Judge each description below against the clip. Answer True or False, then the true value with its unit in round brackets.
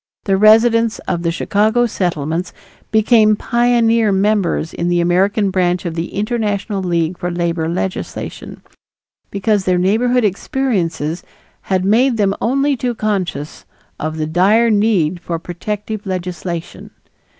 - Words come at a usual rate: False (130 wpm)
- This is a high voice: True (195 Hz)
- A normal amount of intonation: True (3.9 semitones)